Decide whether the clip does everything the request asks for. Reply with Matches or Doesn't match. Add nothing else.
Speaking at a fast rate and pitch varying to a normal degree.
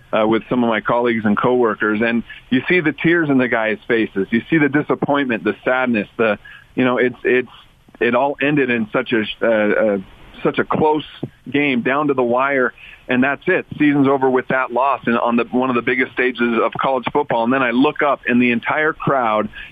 Matches